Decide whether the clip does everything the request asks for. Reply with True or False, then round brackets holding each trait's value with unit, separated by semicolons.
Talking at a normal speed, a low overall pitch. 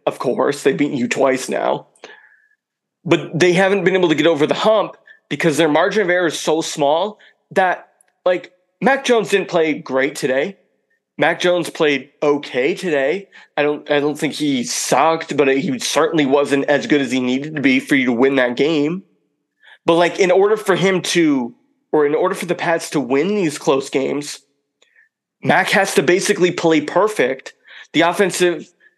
False (180 wpm; 165 Hz)